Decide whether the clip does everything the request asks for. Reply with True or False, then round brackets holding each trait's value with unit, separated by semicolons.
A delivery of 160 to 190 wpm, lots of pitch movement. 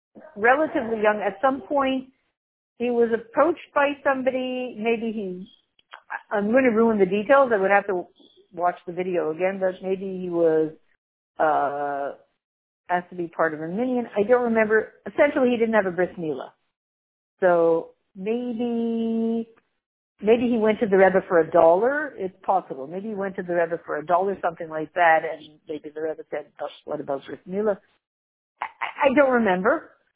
True (170 wpm; 5.8 semitones)